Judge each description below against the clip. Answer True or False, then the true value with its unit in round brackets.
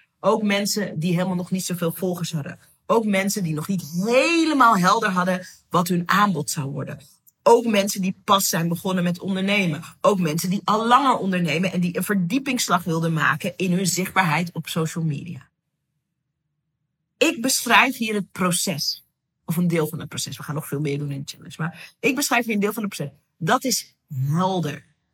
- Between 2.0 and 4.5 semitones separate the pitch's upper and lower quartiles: True (4.2 semitones)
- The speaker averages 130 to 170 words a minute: False (190 wpm)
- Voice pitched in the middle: True (180 Hz)